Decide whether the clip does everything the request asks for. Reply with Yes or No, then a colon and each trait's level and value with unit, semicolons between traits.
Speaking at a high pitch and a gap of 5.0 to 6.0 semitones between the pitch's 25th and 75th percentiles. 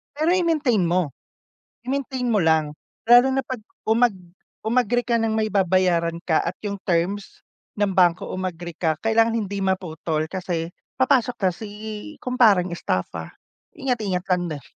Yes: high, 200 Hz; wide, 5.5 semitones